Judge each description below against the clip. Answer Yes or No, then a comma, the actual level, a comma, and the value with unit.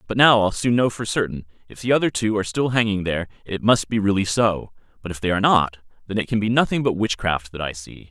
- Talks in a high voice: No, low, 105 Hz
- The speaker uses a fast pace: Yes, fast, 260 wpm